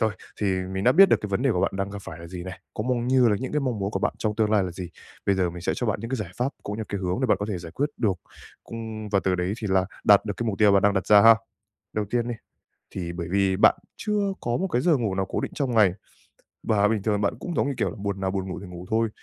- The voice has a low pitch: Yes, low, 105 Hz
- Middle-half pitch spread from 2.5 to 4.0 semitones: Yes, average, 3.5 semitones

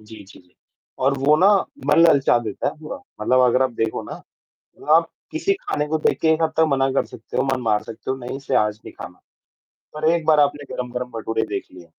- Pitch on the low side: Yes, low, 130 Hz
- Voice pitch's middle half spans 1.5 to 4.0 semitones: No, average, 5.2 semitones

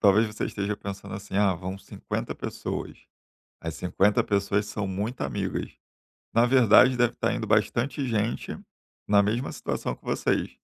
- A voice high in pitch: No, low, 105 Hz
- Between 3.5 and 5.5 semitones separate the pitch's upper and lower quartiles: No, average, 2.8 semitones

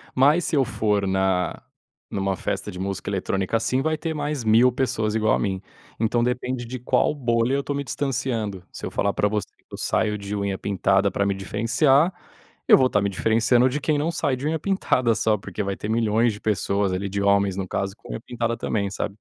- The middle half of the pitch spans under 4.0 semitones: No, average, 4.3 semitones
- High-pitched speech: No, low, 110 Hz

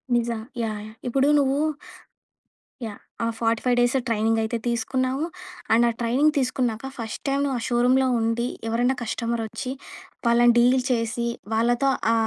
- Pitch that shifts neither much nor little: No, narrow, 2.1 semitones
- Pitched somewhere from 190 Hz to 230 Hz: No, high, 240 Hz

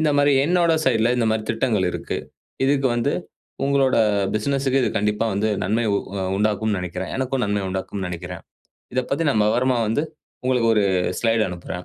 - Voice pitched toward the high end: No, low, 115 Hz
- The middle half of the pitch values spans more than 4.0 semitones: Yes, average, 4.4 semitones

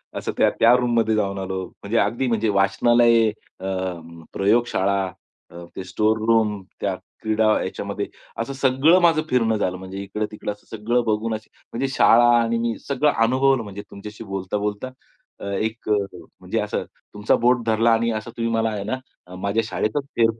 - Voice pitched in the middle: No, low, 110 Hz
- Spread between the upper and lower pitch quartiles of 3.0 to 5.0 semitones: No, narrow, 2.5 semitones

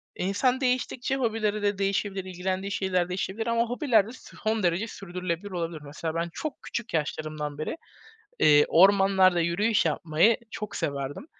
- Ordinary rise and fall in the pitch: Yes, average, 4.6 semitones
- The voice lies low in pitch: No, high, 190 Hz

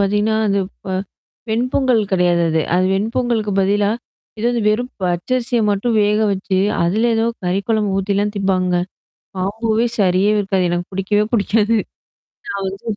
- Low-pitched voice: No, high, 205 Hz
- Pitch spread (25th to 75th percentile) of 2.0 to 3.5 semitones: Yes, average, 2.8 semitones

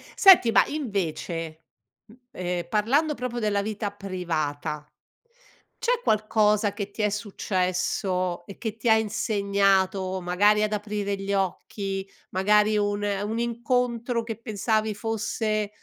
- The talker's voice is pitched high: Yes, high, 205 Hz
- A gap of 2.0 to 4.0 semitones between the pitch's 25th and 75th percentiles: Yes, narrow, 2.5 semitones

